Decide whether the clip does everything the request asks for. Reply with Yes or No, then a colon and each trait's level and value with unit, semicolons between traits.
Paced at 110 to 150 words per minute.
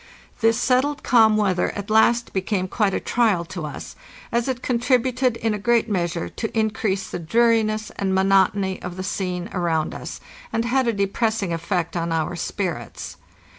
No: average, 175 wpm